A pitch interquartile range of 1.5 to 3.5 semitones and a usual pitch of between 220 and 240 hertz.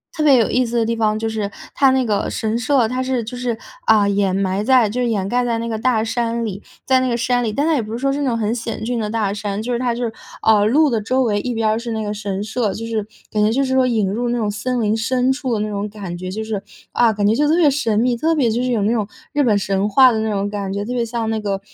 Yes: average, 2.9 semitones; high, 225 Hz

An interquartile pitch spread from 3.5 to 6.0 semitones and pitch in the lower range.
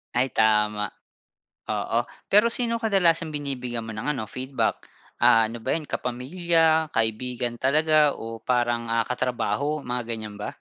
Yes: average, 5.1 semitones; low, 125 Hz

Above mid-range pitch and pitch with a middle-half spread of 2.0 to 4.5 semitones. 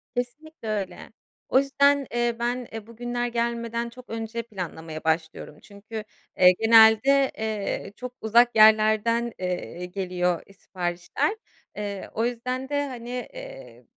Yes: high, 230 Hz; average, 3.4 semitones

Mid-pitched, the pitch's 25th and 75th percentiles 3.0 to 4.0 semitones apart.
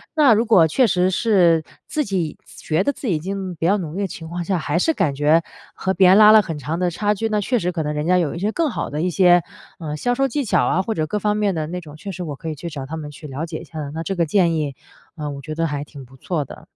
No: medium, 175 Hz; average, 4.4 semitones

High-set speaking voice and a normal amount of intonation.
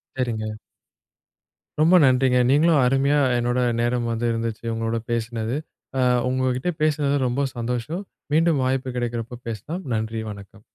No: low, 125 Hz; average, 3.3 semitones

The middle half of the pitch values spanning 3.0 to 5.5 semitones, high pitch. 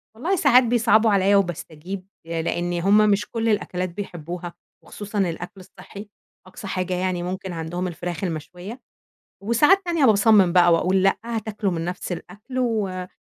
Yes: average, 3.6 semitones; high, 195 Hz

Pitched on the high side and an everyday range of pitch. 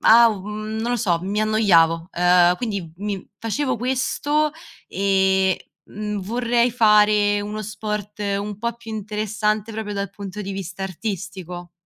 No: high, 210 Hz; narrow, 2.3 semitones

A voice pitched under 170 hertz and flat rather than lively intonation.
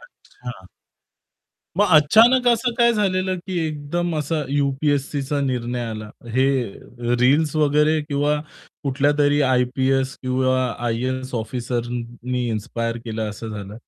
No: low, 135 Hz; average, 3.7 semitones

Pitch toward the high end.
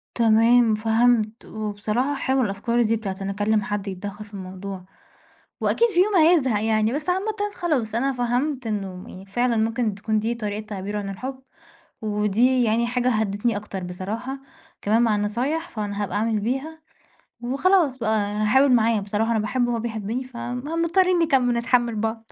Yes: high, 225 Hz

